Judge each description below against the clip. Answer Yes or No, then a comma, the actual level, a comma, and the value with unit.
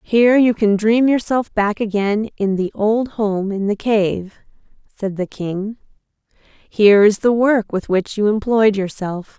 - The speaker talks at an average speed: Yes, average, 165 wpm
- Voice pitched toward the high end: Yes, high, 210 Hz